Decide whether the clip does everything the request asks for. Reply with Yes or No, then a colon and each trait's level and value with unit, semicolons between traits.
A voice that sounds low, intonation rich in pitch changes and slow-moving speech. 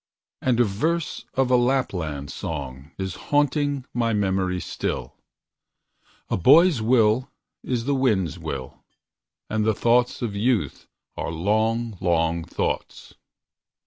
Yes: low, 110 Hz; wide, 5.9 semitones; slow, 120 wpm